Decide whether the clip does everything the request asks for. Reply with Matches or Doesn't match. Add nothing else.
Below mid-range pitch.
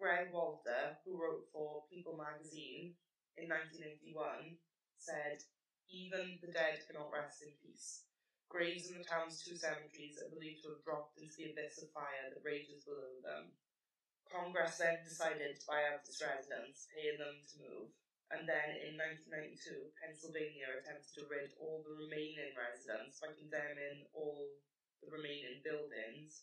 Doesn't match